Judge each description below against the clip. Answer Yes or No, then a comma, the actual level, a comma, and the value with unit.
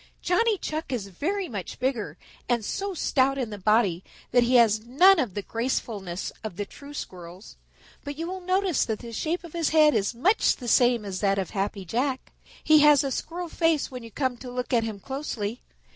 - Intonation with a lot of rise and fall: Yes, wide, 6.5 semitones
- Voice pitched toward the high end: Yes, very high, 250 Hz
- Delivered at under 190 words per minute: No, fast, 205 wpm